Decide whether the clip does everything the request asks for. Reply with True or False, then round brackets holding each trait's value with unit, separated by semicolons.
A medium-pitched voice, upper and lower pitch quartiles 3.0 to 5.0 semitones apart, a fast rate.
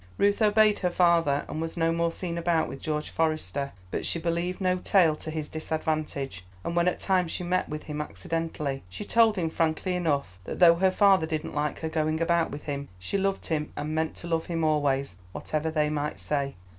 False (160 Hz; 2.4 semitones; 210 wpm)